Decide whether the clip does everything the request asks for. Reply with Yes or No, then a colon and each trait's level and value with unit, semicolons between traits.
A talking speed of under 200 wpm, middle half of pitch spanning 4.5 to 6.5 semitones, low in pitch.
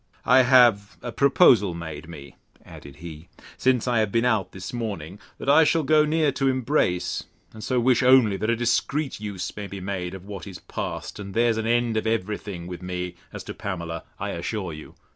No: fast, 205 wpm; wide, 5.4 semitones; low, 105 Hz